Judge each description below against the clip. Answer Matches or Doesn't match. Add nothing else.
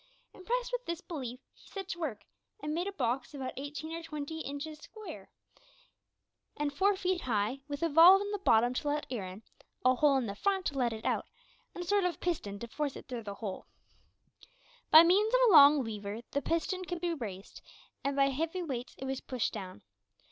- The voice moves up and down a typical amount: Doesn't match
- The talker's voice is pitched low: Doesn't match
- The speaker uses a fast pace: Matches